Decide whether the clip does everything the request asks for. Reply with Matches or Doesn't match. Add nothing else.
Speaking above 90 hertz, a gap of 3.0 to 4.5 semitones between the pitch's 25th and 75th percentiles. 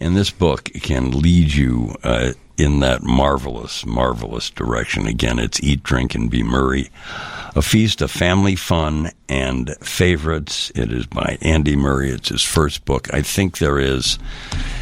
Doesn't match